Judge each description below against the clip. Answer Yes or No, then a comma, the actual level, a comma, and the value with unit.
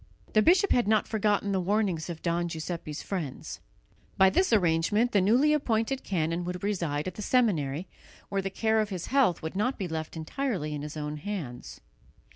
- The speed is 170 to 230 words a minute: Yes, average, 185 wpm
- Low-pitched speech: No, high, 190 Hz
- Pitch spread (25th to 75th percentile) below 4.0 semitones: No, average, 5.1 semitones